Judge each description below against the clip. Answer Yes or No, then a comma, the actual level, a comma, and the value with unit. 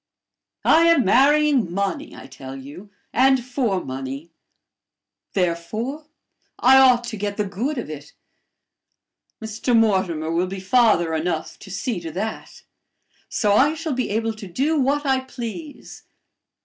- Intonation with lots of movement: Yes, wide, 6.7 semitones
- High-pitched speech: Yes, high, 220 Hz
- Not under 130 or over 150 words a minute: Yes, average, 140 wpm